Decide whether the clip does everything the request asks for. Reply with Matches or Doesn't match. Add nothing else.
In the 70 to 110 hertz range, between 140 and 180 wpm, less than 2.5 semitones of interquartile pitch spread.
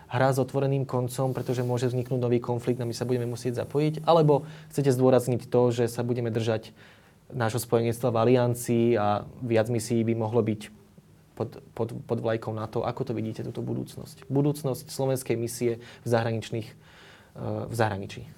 Doesn't match